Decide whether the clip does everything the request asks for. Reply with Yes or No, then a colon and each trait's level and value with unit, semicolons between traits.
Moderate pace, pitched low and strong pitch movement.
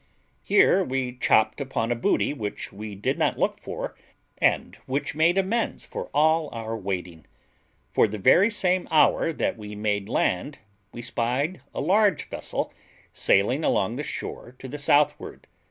Yes: average, 155 wpm; low, 130 Hz; wide, 6.7 semitones